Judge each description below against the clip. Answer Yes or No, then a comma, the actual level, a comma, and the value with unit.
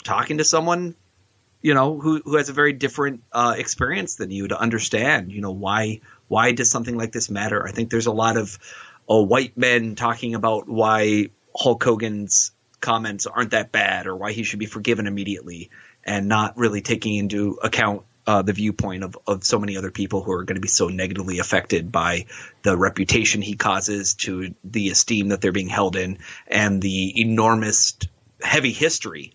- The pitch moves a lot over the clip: No, average, 2.9 semitones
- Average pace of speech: Yes, average, 185 wpm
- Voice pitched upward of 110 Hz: No, low, 105 Hz